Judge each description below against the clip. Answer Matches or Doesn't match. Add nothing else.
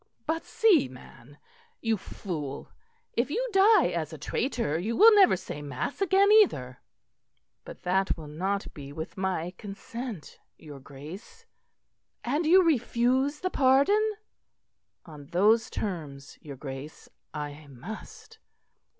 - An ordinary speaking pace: Doesn't match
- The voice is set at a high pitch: Matches